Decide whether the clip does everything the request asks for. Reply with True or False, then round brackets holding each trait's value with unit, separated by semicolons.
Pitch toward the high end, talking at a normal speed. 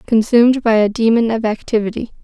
True (225 Hz; 160 wpm)